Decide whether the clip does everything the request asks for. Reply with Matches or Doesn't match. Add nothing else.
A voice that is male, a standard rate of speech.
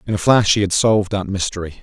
Doesn't match